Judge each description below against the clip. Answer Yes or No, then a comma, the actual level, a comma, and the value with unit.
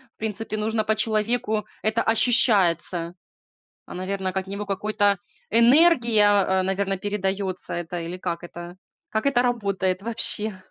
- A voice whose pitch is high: Yes, high, 205 Hz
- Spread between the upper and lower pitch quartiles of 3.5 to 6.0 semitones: No, average, 2.8 semitones